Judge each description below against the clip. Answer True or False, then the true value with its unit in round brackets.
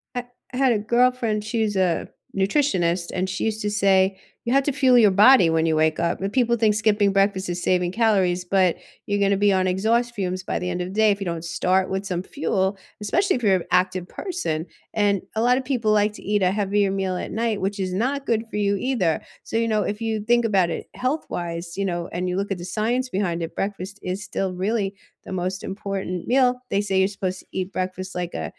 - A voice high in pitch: True (195 Hz)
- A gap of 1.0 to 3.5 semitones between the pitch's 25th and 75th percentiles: True (3.1 semitones)